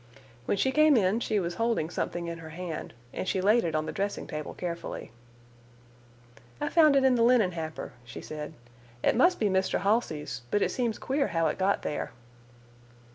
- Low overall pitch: No, high, 190 Hz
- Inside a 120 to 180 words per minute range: No, average, 190 wpm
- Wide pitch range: Yes, wide, 6.3 semitones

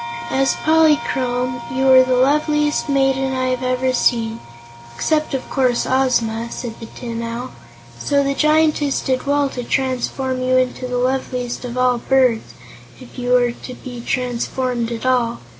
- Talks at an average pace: Yes, average, 160 wpm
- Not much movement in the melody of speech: Yes, narrow, 1.7 semitones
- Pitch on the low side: No, very high, 255 Hz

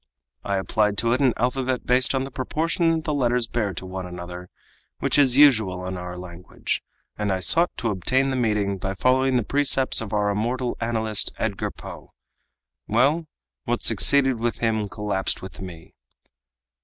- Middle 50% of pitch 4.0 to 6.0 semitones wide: Yes, average, 5.2 semitones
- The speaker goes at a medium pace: Yes, average, 170 wpm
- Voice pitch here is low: Yes, low, 115 Hz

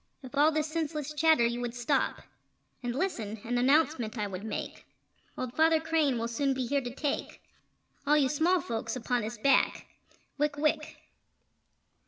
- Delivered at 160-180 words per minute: Yes, average, 165 wpm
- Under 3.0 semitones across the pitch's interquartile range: No, average, 4.3 semitones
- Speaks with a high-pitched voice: Yes, very high, 275 Hz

